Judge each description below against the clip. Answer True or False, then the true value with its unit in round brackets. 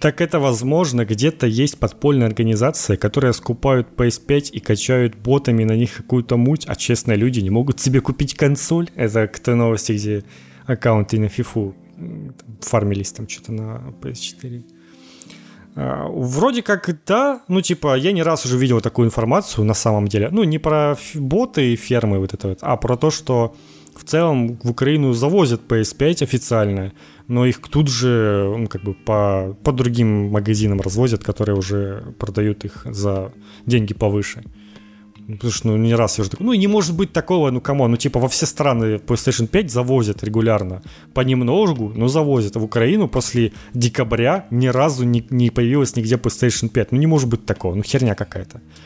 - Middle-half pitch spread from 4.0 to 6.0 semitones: True (4.3 semitones)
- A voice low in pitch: True (120 Hz)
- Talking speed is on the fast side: True (170 wpm)